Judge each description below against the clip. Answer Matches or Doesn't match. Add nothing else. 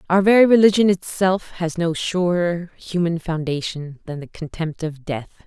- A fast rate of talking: Doesn't match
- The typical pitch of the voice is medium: Matches